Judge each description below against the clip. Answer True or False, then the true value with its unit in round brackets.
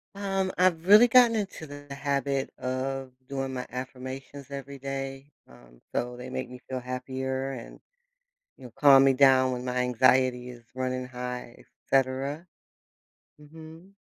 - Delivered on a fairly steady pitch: True (2.1 semitones)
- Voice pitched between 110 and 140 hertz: True (135 Hz)